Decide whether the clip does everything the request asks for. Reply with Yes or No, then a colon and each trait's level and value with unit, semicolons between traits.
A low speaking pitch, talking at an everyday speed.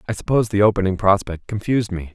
Yes: low, 100 Hz; average, 195 wpm